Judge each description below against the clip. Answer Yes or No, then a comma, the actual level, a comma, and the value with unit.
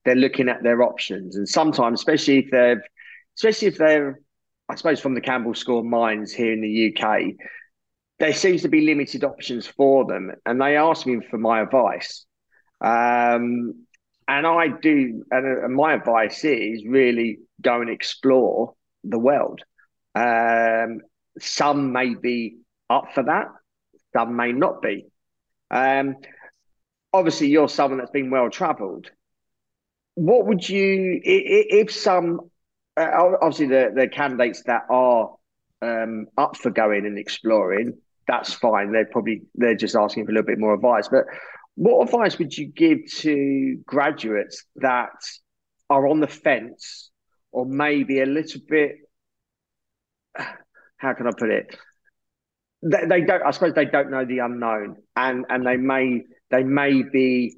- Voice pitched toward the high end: No, low, 130 Hz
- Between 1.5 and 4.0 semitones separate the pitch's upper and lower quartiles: No, average, 4.6 semitones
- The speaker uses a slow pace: No, average, 150 wpm